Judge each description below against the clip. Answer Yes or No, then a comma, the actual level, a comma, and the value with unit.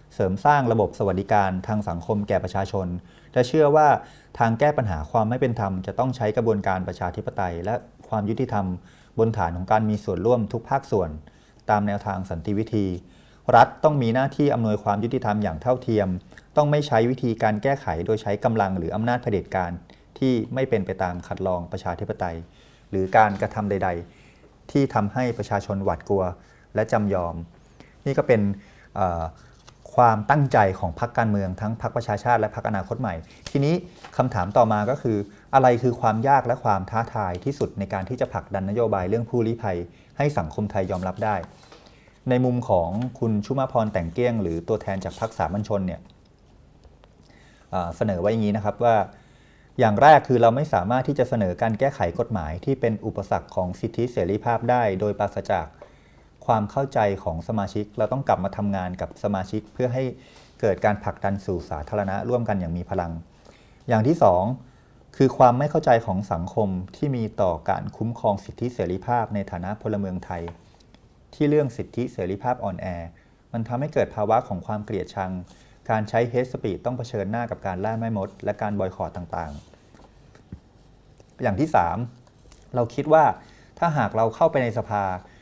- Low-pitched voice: Yes, low, 105 Hz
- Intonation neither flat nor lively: Yes, average, 4.2 semitones